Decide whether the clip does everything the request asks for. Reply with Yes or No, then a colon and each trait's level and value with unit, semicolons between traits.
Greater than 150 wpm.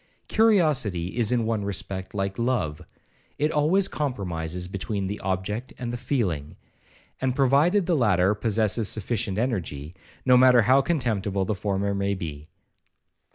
No: average, 140 wpm